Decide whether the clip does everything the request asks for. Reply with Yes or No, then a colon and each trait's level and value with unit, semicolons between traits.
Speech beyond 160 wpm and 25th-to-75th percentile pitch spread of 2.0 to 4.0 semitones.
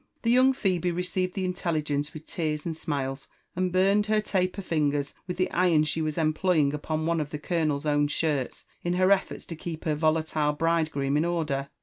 Yes: average, 200 wpm; average, 3.3 semitones